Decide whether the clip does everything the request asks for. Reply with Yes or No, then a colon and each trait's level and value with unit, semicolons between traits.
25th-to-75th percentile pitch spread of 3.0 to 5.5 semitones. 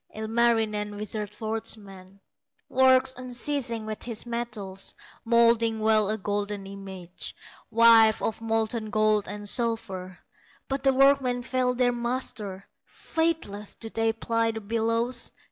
No: narrow, 2.4 semitones